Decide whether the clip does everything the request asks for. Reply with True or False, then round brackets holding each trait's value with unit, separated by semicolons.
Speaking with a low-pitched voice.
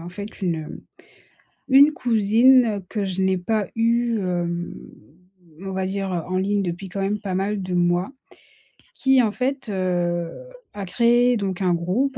False (195 Hz)